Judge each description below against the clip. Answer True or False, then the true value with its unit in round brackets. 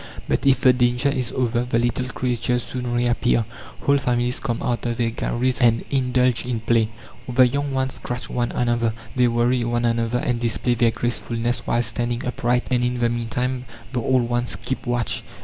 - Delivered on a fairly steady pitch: True (1.0 semitones)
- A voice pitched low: True (120 Hz)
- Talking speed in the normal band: True (185 wpm)